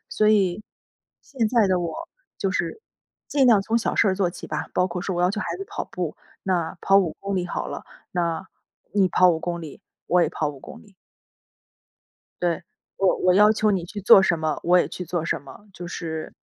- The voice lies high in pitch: No, medium, 180 Hz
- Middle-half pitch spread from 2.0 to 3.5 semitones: Yes, narrow, 2.6 semitones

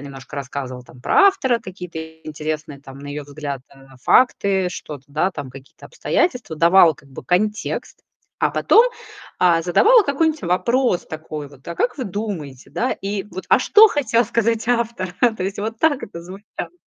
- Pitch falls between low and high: Yes, medium, 180 Hz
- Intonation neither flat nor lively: No, wide, 8.2 semitones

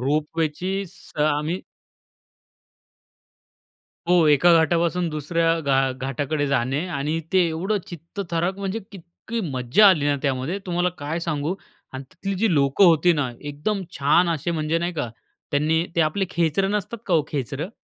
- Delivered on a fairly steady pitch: No, average, 3.6 semitones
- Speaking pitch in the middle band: Yes, medium, 165 Hz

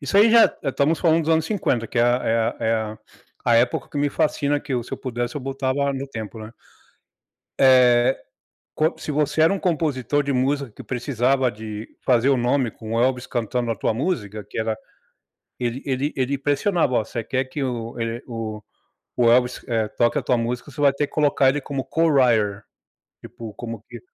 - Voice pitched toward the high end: No, low, 130 Hz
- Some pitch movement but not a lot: Yes, average, 3.4 semitones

